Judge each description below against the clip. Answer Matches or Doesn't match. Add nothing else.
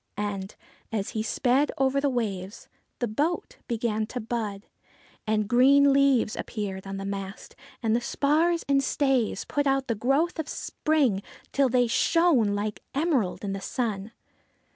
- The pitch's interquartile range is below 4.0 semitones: Doesn't match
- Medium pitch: Doesn't match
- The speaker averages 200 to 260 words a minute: Doesn't match